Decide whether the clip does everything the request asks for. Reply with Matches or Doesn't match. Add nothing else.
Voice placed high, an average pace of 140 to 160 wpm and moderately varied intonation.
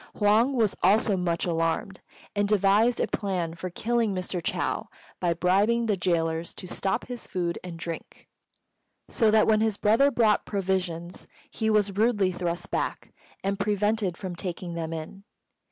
Matches